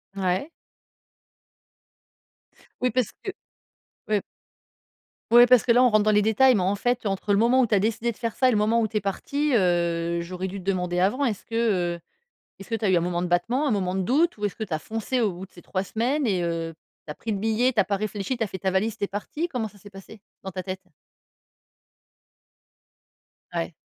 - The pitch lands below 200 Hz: No, high, 205 Hz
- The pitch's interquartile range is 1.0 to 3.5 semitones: No, average, 3.9 semitones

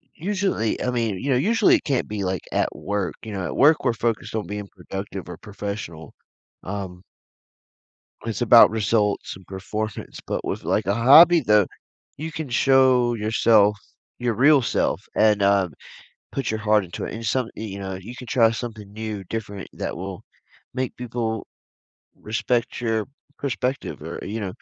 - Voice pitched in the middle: No, low, 110 Hz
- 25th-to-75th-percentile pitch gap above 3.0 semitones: Yes, average, 3.7 semitones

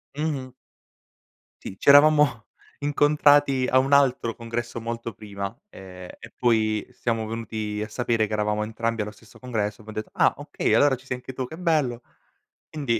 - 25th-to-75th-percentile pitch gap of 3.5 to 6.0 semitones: Yes, average, 3.8 semitones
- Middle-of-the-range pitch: No, low, 115 Hz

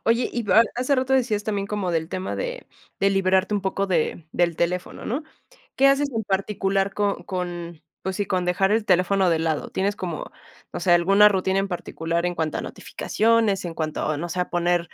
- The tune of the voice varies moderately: Yes, average, 3.1 semitones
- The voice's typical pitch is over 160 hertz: Yes, high, 190 Hz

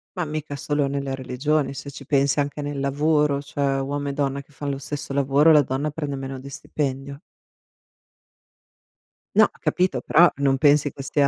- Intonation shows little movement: Yes, narrow, 1.4 semitones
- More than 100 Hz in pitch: Yes, medium, 140 Hz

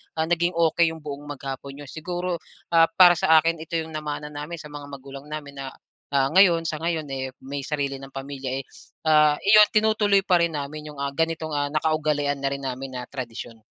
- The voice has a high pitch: No, medium, 150 Hz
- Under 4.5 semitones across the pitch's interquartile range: Yes, average, 2.9 semitones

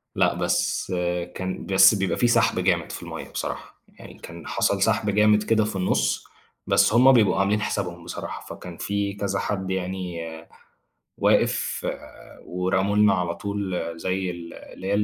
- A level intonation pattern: Yes, narrow, 2.3 semitones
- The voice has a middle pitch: No, very low, 95 Hz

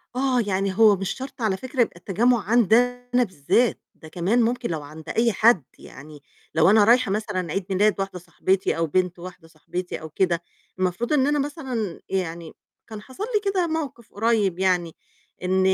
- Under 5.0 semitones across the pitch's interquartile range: No, average, 5.3 semitones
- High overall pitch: Yes, high, 200 Hz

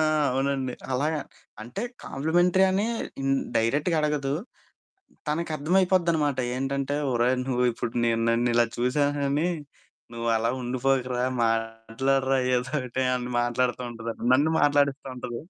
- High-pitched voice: No, low, 135 Hz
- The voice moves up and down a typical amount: Yes, average, 3.2 semitones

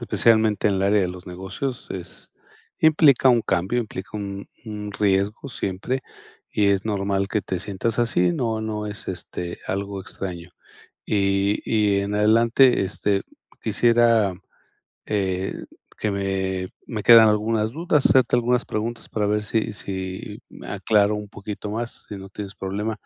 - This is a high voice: No, low, 105 Hz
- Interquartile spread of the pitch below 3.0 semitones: Yes, narrow, 2.5 semitones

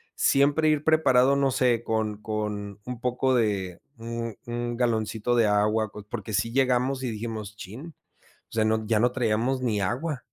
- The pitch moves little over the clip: No, average, 3.1 semitones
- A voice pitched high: No, low, 115 Hz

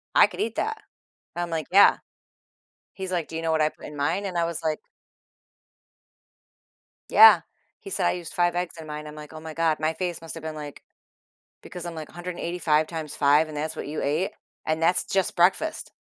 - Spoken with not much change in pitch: Yes, narrow, 2.3 semitones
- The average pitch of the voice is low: No, medium, 165 Hz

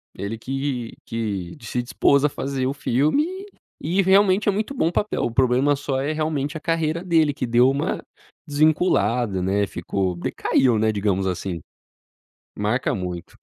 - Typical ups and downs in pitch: No, wide, 6.6 semitones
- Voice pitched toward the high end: No, low, 130 Hz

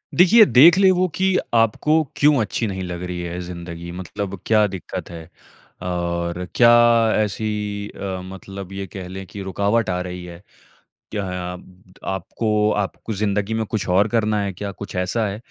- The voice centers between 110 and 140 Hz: No, low, 100 Hz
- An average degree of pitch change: Yes, average, 3.3 semitones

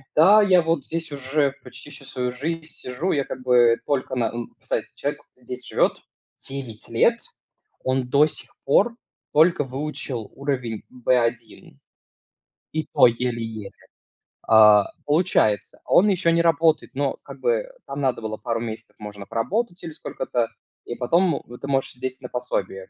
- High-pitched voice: No, low, 130 Hz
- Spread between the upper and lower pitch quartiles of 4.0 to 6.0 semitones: Yes, average, 5.0 semitones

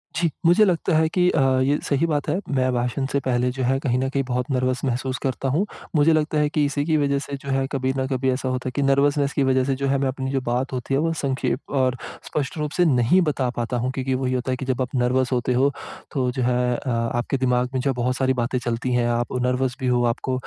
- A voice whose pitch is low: Yes, low, 130 Hz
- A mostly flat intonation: Yes, narrow, 1.9 semitones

